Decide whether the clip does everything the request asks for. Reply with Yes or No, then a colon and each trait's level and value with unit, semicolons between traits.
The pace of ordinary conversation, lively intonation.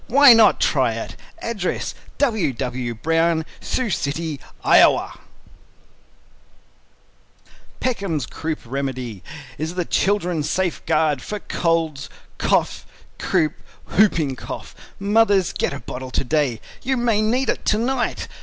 No: slow, 120 wpm; wide, 7.2 semitones